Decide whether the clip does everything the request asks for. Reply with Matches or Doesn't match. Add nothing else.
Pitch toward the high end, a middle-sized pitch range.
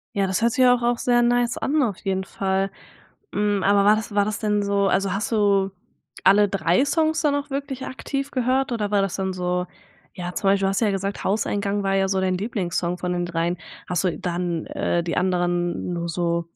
Matches